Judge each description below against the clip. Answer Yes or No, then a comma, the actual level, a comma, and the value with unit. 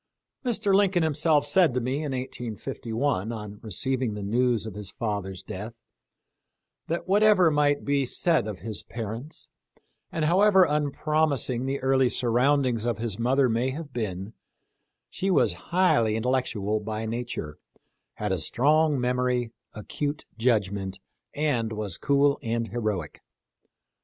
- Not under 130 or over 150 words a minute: Yes, slow, 135 wpm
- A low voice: Yes, low, 125 Hz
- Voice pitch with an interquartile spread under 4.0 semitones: No, average, 5.0 semitones